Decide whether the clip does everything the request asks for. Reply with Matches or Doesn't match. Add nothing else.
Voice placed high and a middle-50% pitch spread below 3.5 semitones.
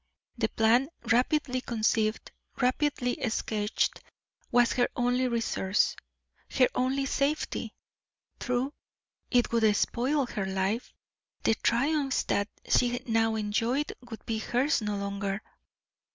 Matches